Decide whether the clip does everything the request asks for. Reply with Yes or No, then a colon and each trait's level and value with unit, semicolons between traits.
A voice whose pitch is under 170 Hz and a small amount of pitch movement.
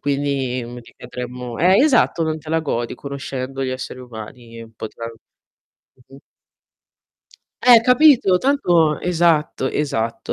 No: medium, 140 Hz; wide, 5.5 semitones